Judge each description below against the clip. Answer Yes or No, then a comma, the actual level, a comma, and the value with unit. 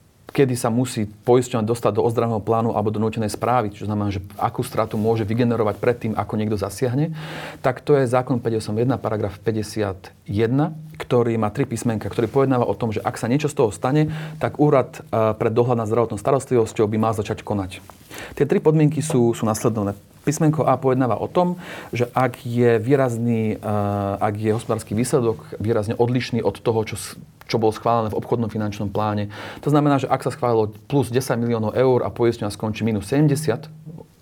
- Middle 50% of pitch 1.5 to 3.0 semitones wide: No, average, 3.4 semitones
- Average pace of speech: No, fast, 180 wpm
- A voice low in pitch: Yes, low, 115 Hz